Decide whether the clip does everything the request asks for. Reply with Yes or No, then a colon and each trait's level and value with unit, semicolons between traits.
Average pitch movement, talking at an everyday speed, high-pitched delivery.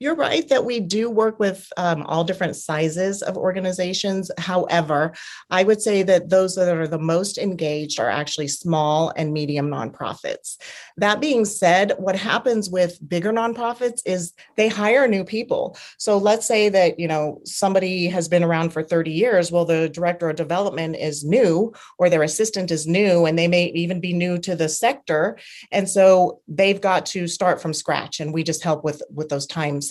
No: average, 3.5 semitones; average, 185 wpm; medium, 180 Hz